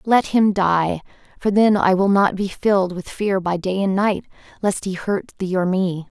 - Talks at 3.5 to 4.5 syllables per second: Yes, 4.4 syllables/s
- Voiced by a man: No, female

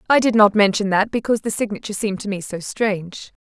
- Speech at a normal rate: No, fast, 225 wpm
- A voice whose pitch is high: Yes, high, 205 Hz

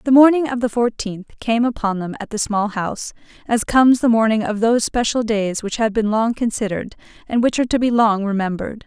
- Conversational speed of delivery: No, fast, 215 wpm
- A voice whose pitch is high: Yes, high, 225 Hz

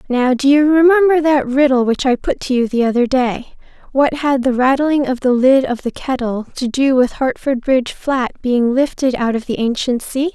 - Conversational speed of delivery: No, fast, 210 wpm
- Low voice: No, very high, 260 Hz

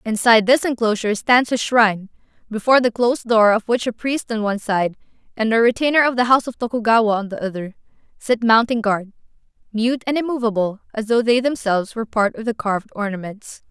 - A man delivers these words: No, female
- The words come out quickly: No, average, 195 wpm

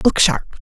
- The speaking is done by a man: No, female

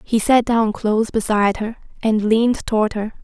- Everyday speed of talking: Yes, average, 185 wpm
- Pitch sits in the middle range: No, high, 220 Hz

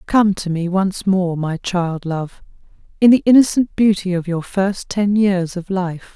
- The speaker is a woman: Yes, female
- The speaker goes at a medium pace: Yes, average, 185 wpm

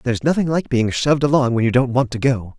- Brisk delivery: Yes, fast, 280 wpm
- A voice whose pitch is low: Yes, low, 130 Hz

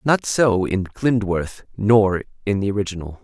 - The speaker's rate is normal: Yes, average, 150 wpm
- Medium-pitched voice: No, low, 105 Hz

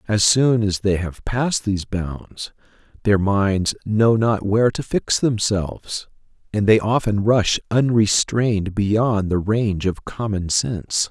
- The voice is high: No, low, 105 Hz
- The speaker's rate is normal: Yes, average, 145 wpm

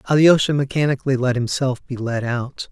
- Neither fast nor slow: Yes, average, 155 wpm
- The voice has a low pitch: Yes, low, 130 Hz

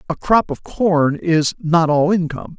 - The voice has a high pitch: No, medium, 170 Hz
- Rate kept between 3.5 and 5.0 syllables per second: Yes, 4.2 syllables/s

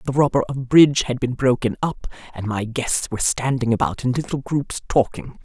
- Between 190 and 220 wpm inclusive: Yes, average, 200 wpm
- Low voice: Yes, low, 125 Hz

